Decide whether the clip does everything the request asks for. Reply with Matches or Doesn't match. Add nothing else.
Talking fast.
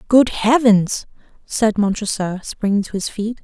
Doesn't match